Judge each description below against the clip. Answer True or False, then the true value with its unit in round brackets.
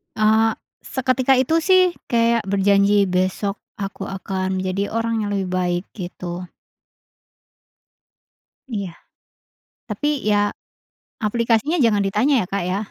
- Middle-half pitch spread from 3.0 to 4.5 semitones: True (3.4 semitones)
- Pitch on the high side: True (205 Hz)